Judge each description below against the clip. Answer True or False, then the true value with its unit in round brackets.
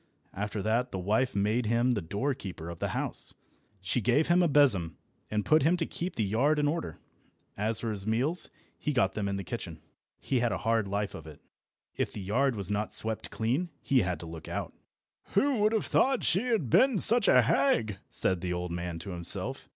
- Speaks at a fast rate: True (215 wpm)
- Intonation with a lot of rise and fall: True (6.8 semitones)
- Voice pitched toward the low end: True (110 Hz)